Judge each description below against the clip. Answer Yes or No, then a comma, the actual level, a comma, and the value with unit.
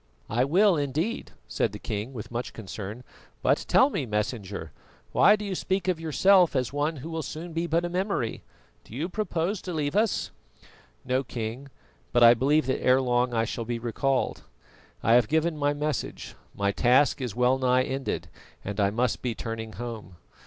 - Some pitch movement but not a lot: No, wide, 5.8 semitones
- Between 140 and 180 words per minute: No, average, 190 wpm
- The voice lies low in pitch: Yes, low, 130 Hz